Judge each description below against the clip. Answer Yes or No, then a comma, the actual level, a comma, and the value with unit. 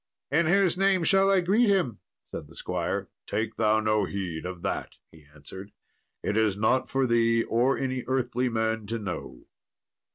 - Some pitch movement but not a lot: No, wide, 5.7 semitones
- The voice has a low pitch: Yes, low, 115 Hz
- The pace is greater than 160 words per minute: Yes, average, 170 wpm